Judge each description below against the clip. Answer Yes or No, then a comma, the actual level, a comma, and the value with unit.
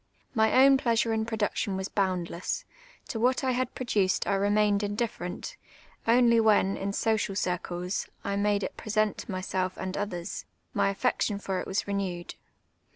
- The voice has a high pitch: Yes, high, 205 Hz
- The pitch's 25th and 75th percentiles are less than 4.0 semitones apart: Yes, average, 2.7 semitones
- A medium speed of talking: Yes, average, 160 wpm